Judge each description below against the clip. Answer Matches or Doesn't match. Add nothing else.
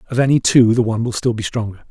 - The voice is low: Matches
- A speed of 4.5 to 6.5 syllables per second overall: Doesn't match